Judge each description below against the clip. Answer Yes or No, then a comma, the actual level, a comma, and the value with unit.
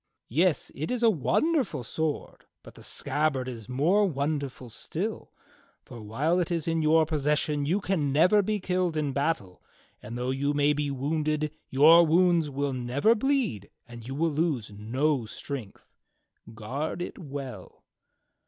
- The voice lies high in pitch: No, medium, 150 Hz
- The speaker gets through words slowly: No, average, 155 wpm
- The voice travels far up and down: No, average, 4.2 semitones